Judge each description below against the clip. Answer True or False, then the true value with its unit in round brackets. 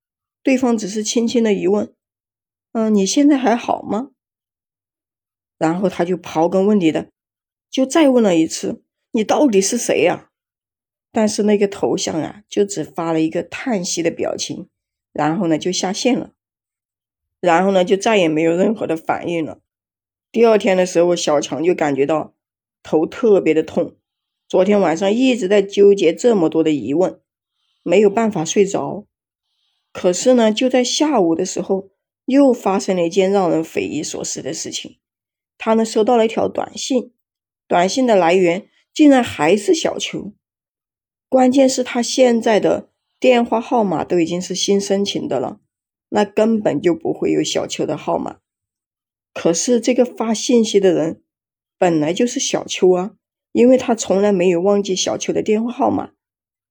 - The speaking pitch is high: True (200 Hz)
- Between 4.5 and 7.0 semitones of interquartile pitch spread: True (5.5 semitones)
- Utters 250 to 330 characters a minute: False (235 characters per minute)